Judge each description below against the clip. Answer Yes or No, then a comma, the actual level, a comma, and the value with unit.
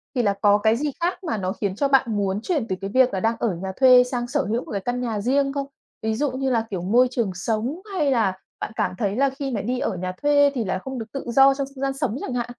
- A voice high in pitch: Yes, high, 245 Hz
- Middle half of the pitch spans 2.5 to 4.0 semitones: No, average, 4.6 semitones